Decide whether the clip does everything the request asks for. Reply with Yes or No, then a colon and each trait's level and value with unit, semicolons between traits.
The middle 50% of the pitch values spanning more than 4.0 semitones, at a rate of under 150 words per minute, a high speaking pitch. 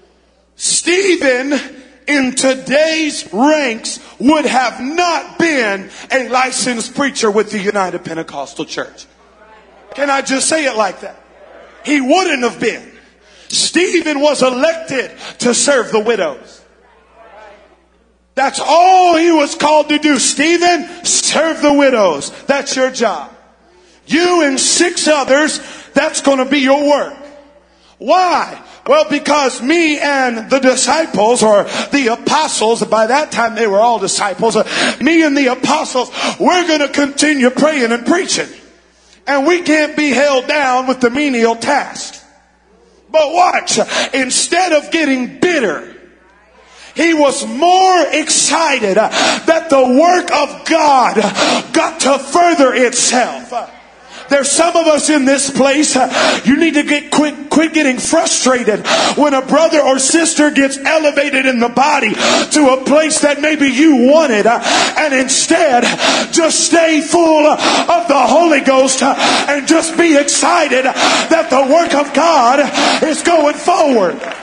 No: average, 3.5 semitones; slow, 135 wpm; very high, 285 Hz